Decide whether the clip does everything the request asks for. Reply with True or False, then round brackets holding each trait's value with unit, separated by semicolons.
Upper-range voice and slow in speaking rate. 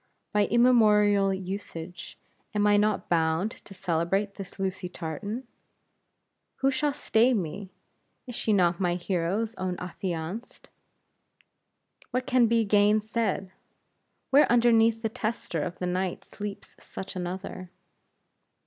True (200 Hz; 120 wpm)